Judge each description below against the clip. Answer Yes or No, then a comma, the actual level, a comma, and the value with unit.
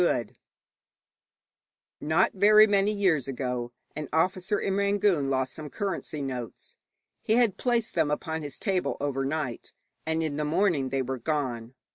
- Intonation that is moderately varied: No, wide, 6.5 semitones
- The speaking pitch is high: No, medium, 155 Hz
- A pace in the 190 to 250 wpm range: No, average, 145 wpm